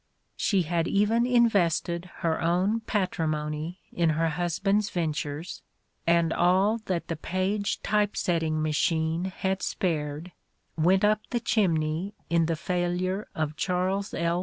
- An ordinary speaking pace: No, slow, 130 wpm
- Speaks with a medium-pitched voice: Yes, medium, 175 Hz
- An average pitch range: Yes, average, 3.3 semitones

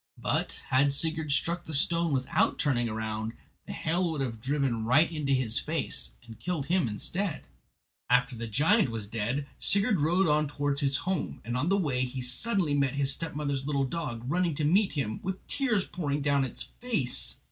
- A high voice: No, medium, 145 Hz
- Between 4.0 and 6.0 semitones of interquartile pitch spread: Yes, average, 4.8 semitones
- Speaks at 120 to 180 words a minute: No, average, 190 wpm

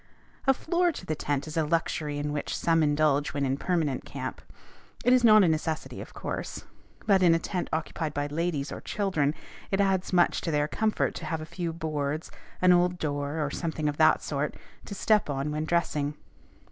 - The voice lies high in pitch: No, medium, 160 Hz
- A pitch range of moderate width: Yes, average, 3.4 semitones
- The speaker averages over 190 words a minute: Yes, average, 200 wpm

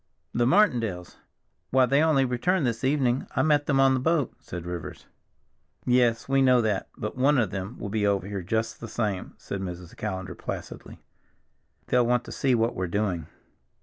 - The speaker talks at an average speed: Yes, average, 180 wpm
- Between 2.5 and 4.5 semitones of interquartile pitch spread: No, average, 5.0 semitones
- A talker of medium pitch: No, low, 115 Hz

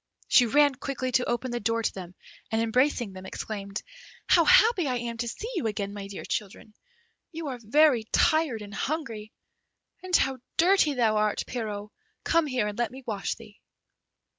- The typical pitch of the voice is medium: No, high, 235 Hz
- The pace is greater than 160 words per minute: Yes, average, 180 wpm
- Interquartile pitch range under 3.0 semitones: No, average, 5.2 semitones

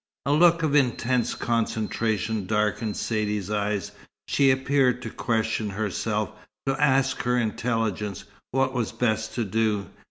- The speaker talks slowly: Yes, slow, 130 wpm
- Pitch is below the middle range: Yes, low, 115 Hz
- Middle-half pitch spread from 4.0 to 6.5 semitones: No, average, 3.4 semitones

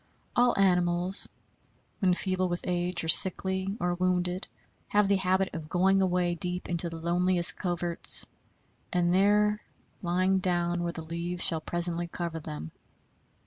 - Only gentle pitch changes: Yes, narrow, 1.5 semitones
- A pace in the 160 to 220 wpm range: No, average, 145 wpm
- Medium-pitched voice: Yes, medium, 180 Hz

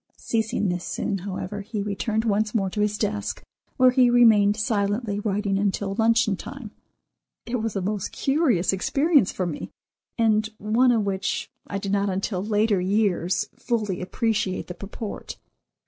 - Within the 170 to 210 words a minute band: No, average, 155 wpm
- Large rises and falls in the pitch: No, narrow, 2.4 semitones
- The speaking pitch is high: Yes, high, 210 Hz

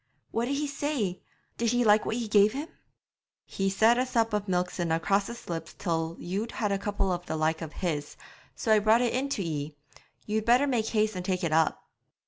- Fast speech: Yes, fast, 220 wpm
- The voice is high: Yes, high, 205 Hz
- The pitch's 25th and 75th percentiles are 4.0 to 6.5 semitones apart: Yes, average, 5.0 semitones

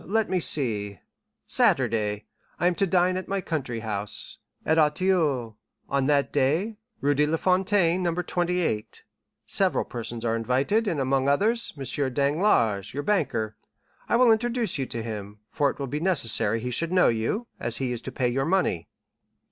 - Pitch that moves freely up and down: Yes, wide, 7.6 semitones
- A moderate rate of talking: Yes, average, 165 wpm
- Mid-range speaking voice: Yes, medium, 145 Hz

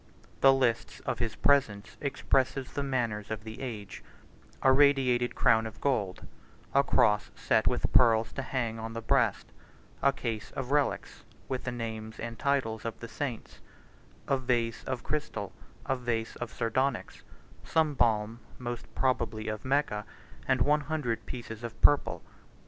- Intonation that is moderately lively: Yes, average, 3.2 semitones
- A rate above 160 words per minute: No, average, 150 wpm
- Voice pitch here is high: No, low, 120 Hz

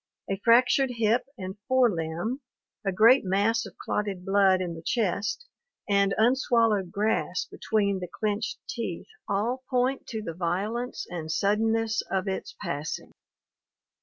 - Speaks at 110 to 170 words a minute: Yes, slow, 135 wpm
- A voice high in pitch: Yes, high, 210 Hz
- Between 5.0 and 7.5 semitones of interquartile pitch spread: No, average, 3.5 semitones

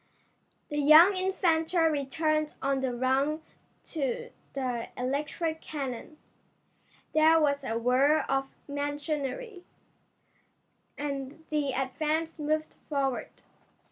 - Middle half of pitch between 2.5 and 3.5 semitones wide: Yes, average, 2.8 semitones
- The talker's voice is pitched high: Yes, very high, 295 Hz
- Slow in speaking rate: Yes, slow, 95 wpm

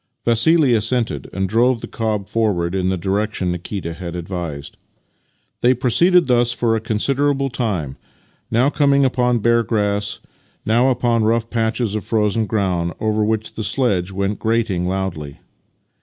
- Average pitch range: Yes, average, 4.0 semitones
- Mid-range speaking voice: No, low, 110 Hz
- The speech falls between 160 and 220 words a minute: No, average, 145 wpm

